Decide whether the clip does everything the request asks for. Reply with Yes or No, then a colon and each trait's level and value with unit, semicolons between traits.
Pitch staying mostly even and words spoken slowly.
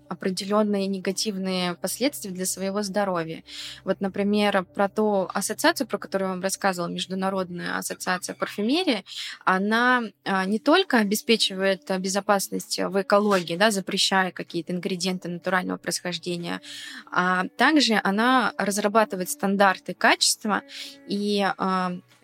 Yes: narrow, 2.1 semitones; slow, 105 wpm